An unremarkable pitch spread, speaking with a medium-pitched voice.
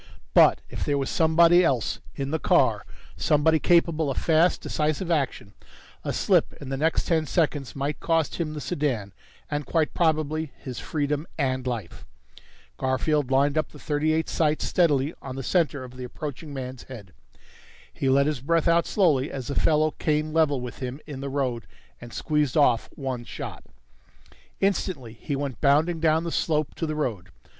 Yes: average, 3.2 semitones; medium, 145 Hz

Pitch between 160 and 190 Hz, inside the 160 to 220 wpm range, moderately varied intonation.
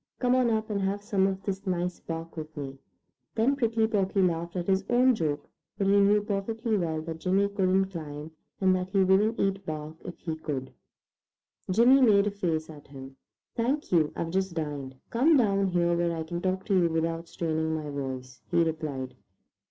Yes: medium, 185 Hz; average, 195 wpm; average, 4.1 semitones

